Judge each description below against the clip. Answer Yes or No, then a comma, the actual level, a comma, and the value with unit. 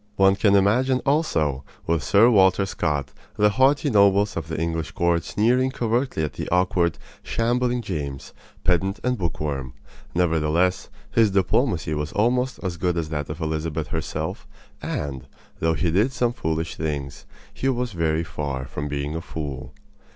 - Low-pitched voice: Yes, very low, 85 Hz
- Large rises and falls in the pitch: Yes, wide, 5.8 semitones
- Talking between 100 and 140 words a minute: No, average, 155 wpm